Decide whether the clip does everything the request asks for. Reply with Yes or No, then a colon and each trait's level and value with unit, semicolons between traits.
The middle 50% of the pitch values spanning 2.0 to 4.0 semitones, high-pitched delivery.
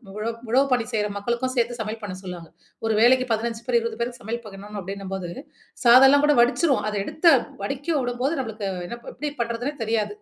Yes: average, 3.3 semitones; high, 235 Hz